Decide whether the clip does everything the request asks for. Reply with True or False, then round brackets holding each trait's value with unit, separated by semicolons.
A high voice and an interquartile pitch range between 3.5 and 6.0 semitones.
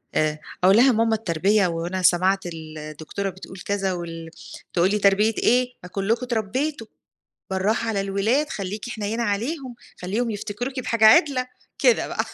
True (205 Hz; 4.0 semitones)